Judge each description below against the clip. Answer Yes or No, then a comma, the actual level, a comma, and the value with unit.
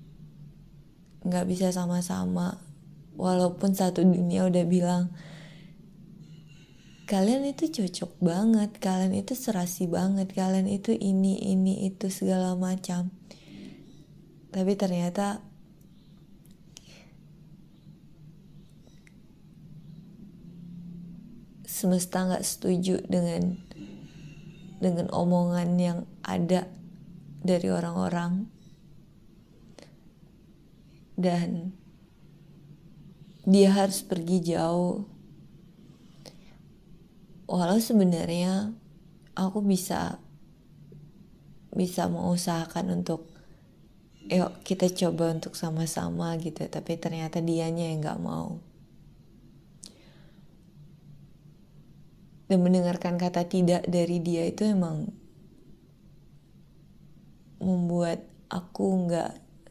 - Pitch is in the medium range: Yes, medium, 180 Hz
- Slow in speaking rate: Yes, slow, 70 wpm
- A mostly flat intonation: Yes, narrow, 1.8 semitones